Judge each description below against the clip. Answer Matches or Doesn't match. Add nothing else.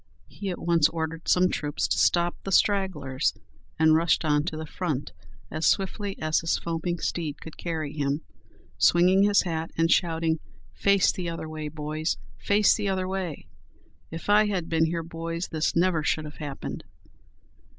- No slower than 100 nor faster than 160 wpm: Doesn't match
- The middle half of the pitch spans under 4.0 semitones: Matches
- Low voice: Doesn't match